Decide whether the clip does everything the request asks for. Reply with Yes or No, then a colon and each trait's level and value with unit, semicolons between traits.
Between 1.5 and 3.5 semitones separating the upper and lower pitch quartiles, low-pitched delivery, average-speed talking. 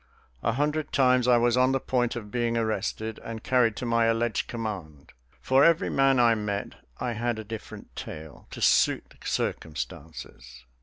Yes: average, 3.1 semitones; low, 115 Hz; average, 170 wpm